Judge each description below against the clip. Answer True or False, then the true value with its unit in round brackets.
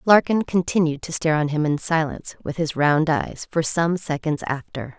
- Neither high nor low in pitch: True (160 Hz)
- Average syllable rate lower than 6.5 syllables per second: True (5.0 syllables/s)